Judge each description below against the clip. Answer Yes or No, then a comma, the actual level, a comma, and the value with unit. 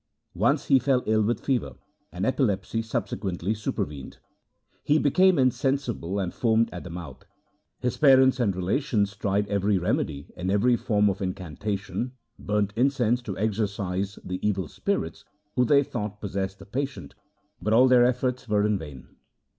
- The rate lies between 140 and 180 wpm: Yes, average, 155 wpm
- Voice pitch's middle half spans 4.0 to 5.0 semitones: Yes, average, 4.5 semitones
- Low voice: Yes, low, 105 Hz